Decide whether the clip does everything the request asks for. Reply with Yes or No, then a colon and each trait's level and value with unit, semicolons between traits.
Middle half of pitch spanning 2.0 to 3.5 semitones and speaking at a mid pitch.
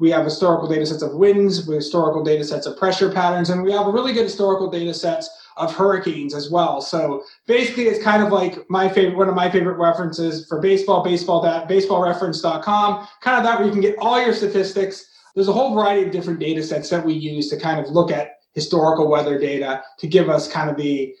No: average, 4.0 semitones; medium, 175 Hz